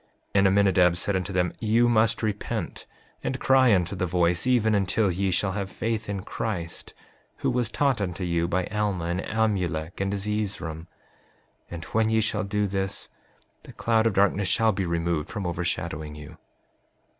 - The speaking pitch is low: Yes, low, 100 Hz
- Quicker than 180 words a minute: No, average, 170 wpm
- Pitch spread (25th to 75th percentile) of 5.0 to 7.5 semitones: No, average, 3.6 semitones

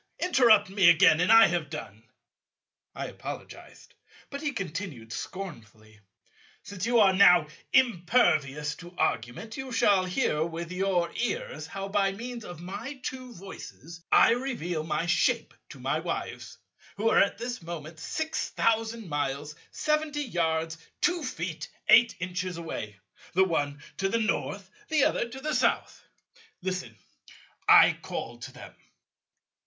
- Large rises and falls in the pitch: Yes, wide, 6.4 semitones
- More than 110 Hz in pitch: Yes, medium, 185 Hz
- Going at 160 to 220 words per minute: No, average, 140 wpm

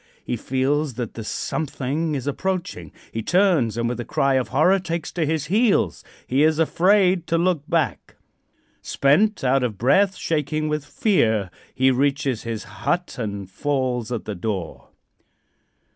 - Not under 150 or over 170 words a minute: Yes, average, 155 wpm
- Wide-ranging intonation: Yes, wide, 5.7 semitones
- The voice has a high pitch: No, medium, 140 Hz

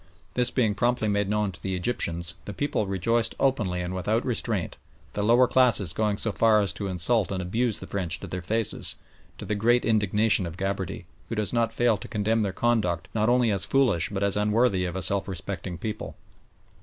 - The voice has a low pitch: Yes, low, 105 Hz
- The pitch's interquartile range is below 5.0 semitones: Yes, average, 3.5 semitones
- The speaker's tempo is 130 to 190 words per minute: No, fast, 205 wpm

